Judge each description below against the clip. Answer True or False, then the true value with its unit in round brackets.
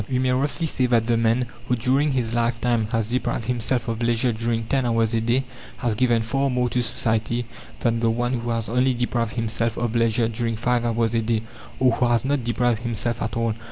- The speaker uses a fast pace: True (220 wpm)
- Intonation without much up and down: True (1.5 semitones)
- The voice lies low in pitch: True (120 Hz)